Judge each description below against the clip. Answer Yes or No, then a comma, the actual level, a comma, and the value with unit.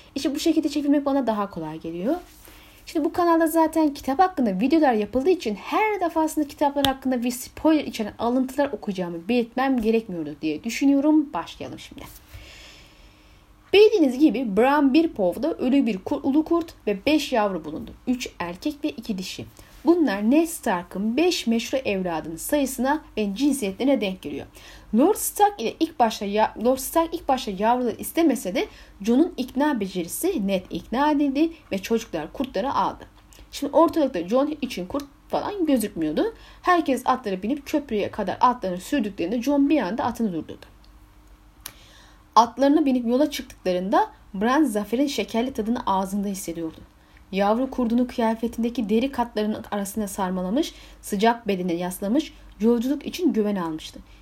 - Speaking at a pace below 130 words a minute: No, fast, 140 wpm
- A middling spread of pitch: No, wide, 6.3 semitones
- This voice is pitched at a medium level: No, very high, 250 Hz